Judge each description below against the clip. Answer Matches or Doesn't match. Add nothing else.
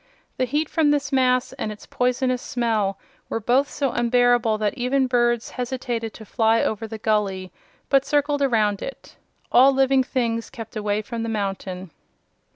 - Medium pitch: Doesn't match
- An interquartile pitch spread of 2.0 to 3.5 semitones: Matches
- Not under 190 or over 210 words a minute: Doesn't match